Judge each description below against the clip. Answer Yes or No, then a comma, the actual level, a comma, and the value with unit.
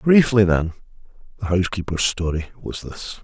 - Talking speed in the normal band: No, slow, 130 wpm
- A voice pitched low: Yes, low, 100 Hz